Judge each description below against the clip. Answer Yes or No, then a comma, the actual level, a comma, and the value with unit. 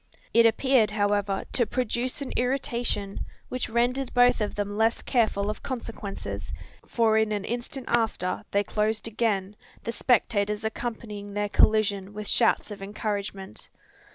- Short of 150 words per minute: Yes, average, 140 wpm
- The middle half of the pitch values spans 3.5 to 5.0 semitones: No, average, 2.7 semitones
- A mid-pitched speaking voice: No, high, 220 Hz